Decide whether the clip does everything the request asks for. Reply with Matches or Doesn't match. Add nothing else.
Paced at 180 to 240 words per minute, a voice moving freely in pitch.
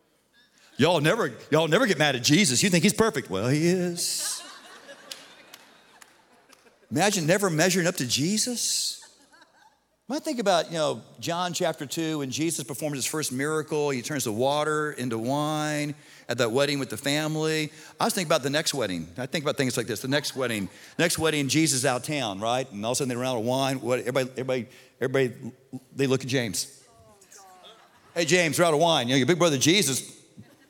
Doesn't match